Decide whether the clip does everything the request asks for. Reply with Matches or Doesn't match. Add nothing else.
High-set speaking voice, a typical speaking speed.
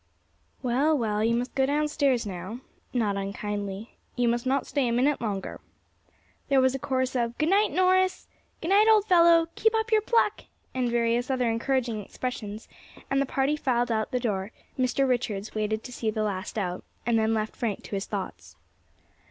Matches